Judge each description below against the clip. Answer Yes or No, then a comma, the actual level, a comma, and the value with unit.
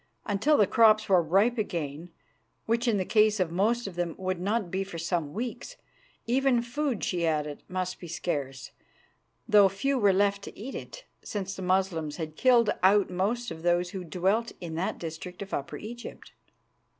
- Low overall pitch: No, high, 195 Hz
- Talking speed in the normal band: Yes, average, 180 wpm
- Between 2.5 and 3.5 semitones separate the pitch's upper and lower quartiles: No, average, 4.3 semitones